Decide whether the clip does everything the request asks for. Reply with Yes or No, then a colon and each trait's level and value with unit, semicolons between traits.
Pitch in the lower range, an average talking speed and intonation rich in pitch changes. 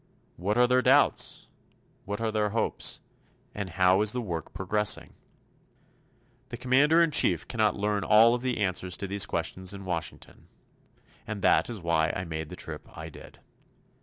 No: low, 105 Hz; average, 165 wpm; average, 4.1 semitones